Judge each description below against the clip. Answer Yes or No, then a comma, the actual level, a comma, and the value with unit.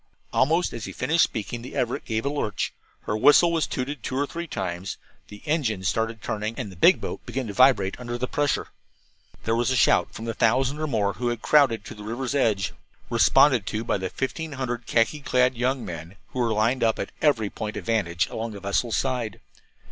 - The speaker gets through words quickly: Yes, fast, 215 wpm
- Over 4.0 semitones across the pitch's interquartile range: No, average, 3.7 semitones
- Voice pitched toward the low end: Yes, low, 120 Hz